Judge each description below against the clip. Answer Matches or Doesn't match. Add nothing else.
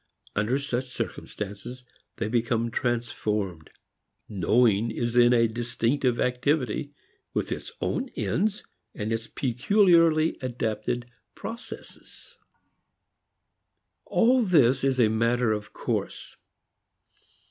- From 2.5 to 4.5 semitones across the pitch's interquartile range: Matches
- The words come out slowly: Matches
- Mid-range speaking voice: Doesn't match